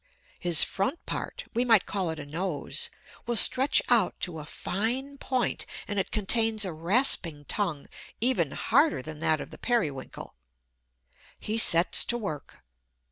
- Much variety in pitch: Yes, wide, 6.8 semitones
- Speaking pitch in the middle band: No, high, 195 Hz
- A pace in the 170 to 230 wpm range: No, average, 150 wpm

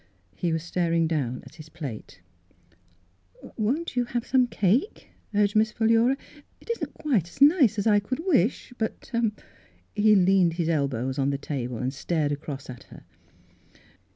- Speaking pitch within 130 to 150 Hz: No, medium, 185 Hz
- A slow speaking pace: No, average, 170 wpm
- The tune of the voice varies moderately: No, wide, 8.0 semitones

